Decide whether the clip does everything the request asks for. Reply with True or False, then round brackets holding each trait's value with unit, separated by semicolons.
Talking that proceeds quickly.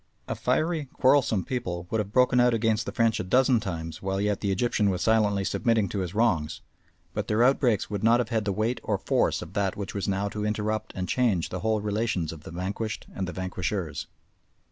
True (215 wpm)